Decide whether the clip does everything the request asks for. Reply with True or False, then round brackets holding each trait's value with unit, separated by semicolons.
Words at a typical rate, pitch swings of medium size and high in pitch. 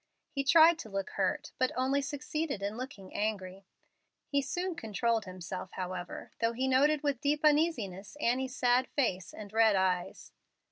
False (155 wpm; 6.5 semitones; 245 Hz)